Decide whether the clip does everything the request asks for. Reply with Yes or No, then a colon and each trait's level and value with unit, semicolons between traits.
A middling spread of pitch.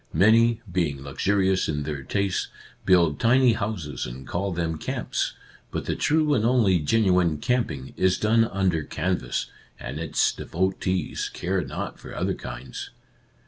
No: wide, 5.8 semitones